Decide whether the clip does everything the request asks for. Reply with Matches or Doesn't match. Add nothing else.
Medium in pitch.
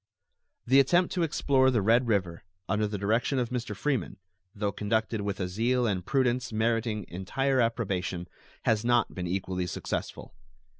Doesn't match